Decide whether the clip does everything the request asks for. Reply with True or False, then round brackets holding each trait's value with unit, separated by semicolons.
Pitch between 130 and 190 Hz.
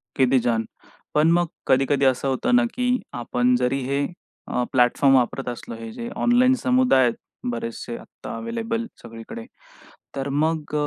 True (135 Hz)